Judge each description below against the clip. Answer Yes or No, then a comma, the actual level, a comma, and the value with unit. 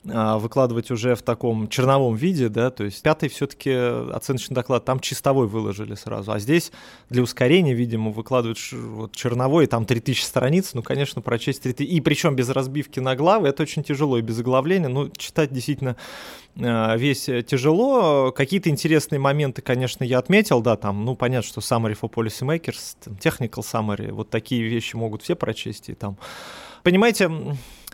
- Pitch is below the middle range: Yes, low, 125 Hz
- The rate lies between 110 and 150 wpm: No, fast, 160 wpm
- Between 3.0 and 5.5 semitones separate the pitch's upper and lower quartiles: Yes, average, 3.6 semitones